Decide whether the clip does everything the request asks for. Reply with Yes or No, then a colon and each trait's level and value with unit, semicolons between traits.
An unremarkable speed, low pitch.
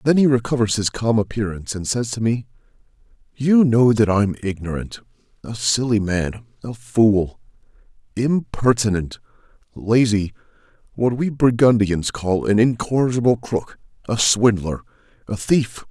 No: slow, 115 wpm; low, 110 Hz